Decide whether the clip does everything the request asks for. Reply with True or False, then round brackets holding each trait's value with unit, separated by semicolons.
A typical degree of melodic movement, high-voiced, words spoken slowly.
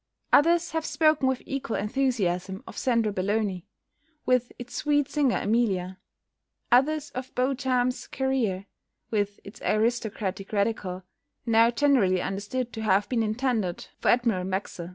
True (4.8 semitones; 230 Hz; 130 wpm)